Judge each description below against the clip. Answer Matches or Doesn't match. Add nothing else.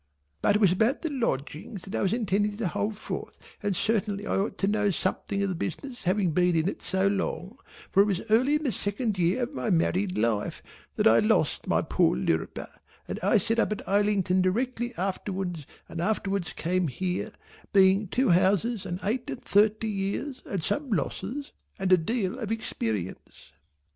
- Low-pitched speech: Doesn't match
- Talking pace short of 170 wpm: Doesn't match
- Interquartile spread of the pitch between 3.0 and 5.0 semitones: Matches